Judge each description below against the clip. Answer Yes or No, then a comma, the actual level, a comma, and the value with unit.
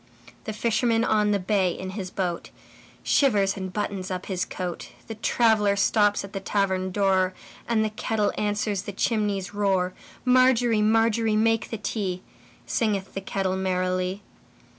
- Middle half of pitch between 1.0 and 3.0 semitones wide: Yes, narrow, 2.5 semitones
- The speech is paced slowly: Yes, slow, 130 wpm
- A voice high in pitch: Yes, high, 205 Hz